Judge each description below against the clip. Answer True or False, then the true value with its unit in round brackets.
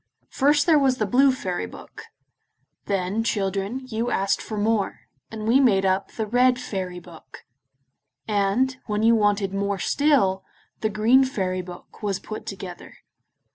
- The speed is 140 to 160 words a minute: True (150 wpm)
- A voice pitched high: True (215 Hz)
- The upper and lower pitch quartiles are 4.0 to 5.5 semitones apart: True (4.4 semitones)